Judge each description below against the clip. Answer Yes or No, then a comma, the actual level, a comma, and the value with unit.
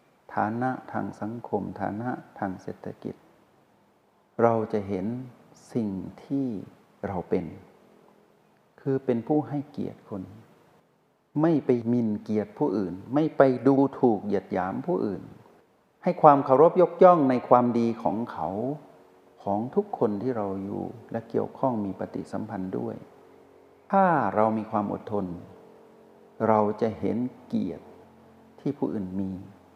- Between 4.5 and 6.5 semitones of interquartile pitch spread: Yes, average, 5.1 semitones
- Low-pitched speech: Yes, low, 115 Hz